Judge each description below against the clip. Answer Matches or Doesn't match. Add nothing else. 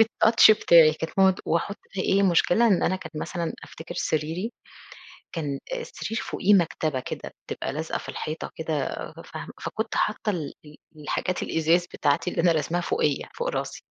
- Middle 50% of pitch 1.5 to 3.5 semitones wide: Doesn't match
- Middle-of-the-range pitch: Matches